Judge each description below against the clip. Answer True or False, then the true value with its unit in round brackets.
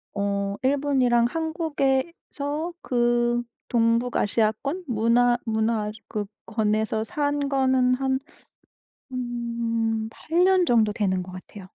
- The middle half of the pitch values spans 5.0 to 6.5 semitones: False (4.3 semitones)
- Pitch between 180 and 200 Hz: False (240 Hz)